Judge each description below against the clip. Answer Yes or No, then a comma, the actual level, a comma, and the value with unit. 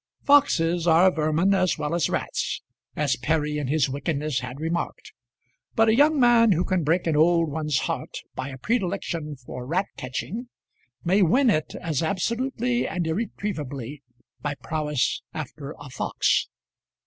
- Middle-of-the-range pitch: Yes, medium, 160 Hz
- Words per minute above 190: No, average, 150 wpm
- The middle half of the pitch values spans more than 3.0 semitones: Yes, average, 4.8 semitones